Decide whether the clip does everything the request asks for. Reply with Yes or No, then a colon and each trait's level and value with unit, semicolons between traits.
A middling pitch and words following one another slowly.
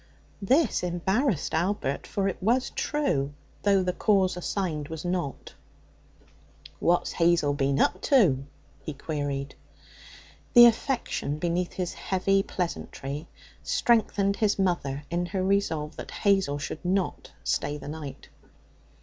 Yes: medium, 175 Hz; slow, 125 wpm